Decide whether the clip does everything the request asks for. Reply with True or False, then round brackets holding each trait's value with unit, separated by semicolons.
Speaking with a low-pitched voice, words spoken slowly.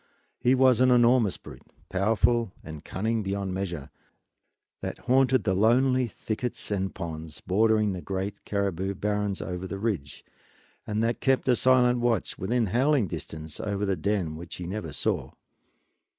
False (105 Hz; 150 wpm)